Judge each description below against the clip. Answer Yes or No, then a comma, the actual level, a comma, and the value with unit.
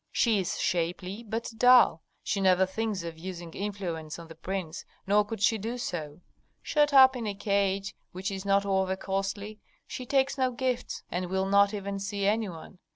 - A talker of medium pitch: No, high, 195 Hz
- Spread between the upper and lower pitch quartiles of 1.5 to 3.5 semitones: Yes, average, 3.0 semitones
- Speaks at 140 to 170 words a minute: No, average, 185 wpm